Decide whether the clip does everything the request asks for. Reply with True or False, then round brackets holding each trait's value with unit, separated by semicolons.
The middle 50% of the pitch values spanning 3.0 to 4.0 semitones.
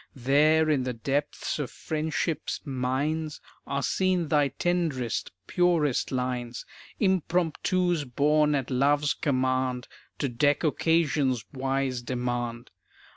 True (3.6 semitones)